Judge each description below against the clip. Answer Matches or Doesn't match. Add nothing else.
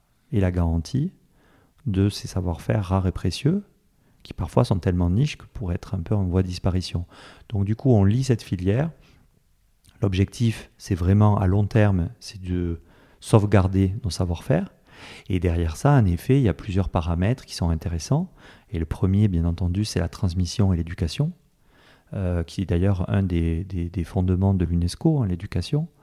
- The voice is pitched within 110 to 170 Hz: Doesn't match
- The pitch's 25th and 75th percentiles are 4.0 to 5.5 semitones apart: Matches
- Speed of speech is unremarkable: Matches